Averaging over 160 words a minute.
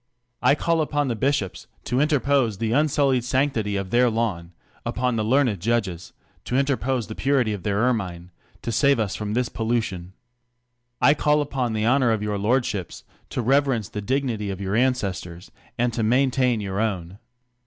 Yes: average, 170 wpm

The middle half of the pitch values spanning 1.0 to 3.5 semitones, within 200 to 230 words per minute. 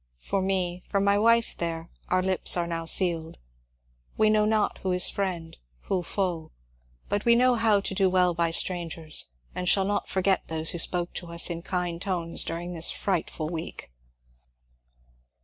No: average, 2.8 semitones; average, 170 wpm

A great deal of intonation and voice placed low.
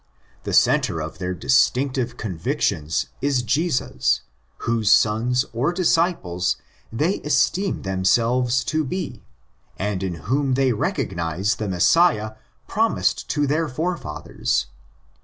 Yes: wide, 7.6 semitones; low, 120 Hz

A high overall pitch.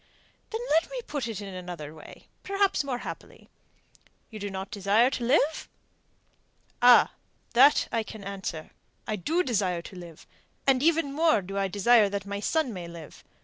Yes: high, 210 Hz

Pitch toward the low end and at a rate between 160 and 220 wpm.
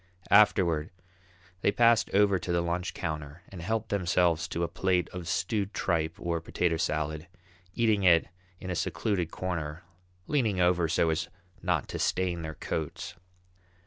No: very low, 90 Hz; average, 150 wpm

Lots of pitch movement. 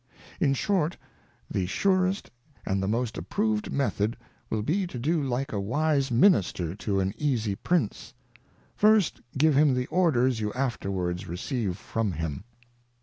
Yes: wide, 7.8 semitones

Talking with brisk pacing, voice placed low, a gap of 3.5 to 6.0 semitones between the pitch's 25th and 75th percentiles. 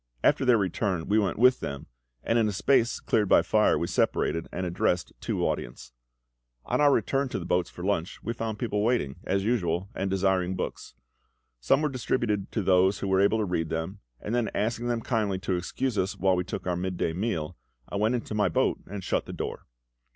Yes: fast, 210 wpm; low, 100 Hz; average, 4.0 semitones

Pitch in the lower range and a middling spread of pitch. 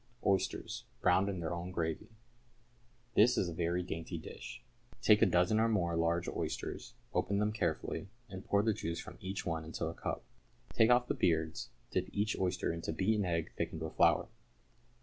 Yes: very low, 90 Hz; average, 3.4 semitones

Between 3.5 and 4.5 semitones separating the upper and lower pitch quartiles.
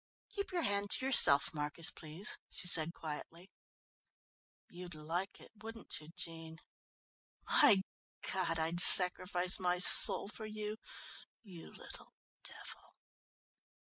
Yes: average, 3.8 semitones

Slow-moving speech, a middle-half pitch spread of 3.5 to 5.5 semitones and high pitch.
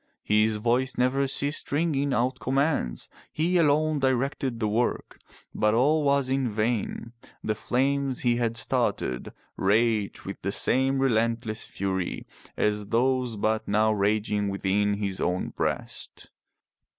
No: slow, 130 wpm; average, 4.2 semitones; low, 115 Hz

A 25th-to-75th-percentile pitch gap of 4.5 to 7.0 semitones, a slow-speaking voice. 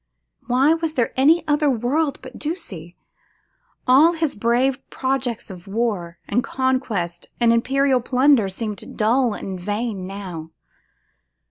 Yes: average, 5.1 semitones; slow, 125 wpm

